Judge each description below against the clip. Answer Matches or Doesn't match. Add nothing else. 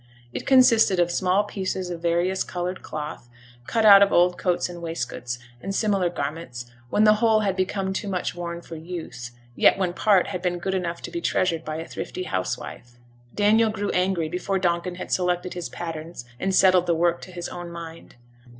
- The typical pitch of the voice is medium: Matches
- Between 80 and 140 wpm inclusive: Doesn't match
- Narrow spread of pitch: Matches